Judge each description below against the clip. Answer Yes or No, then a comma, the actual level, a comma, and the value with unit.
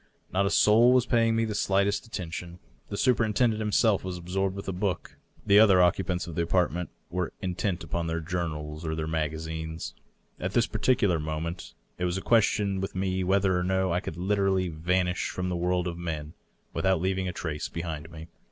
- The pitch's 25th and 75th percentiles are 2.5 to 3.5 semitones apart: Yes, average, 2.8 semitones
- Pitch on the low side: Yes, very low, 90 Hz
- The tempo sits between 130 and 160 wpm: No, average, 195 wpm